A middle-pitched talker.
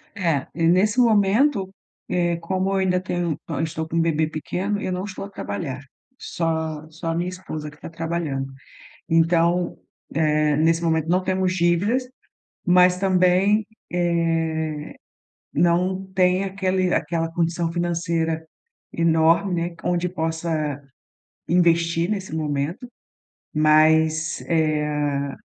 Yes: medium, 170 Hz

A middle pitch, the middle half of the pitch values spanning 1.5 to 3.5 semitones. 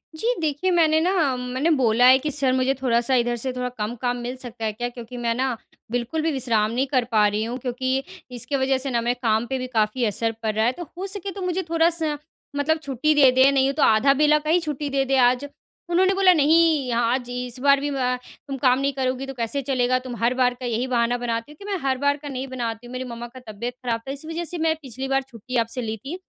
No: very high, 260 Hz; average, 3.0 semitones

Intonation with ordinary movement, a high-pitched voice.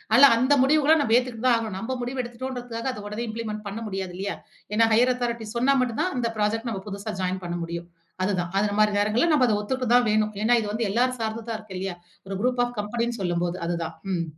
Yes: average, 3.2 semitones; high, 225 Hz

